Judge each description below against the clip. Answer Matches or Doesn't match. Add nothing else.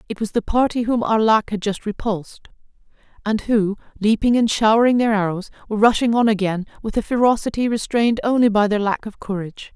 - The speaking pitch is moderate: Doesn't match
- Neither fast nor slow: Matches